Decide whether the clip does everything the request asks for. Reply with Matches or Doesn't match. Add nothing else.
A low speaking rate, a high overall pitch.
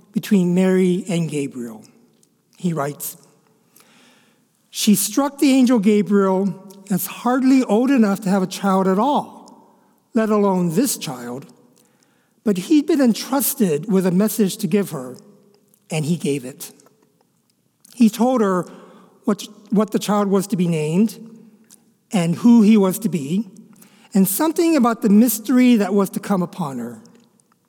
Doesn't match